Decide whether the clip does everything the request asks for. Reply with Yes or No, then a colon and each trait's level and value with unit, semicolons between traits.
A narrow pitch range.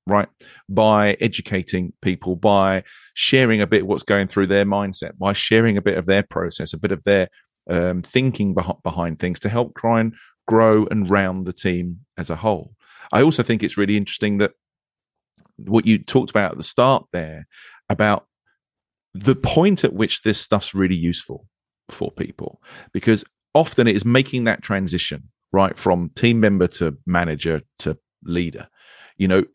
No: average, 3.5 semitones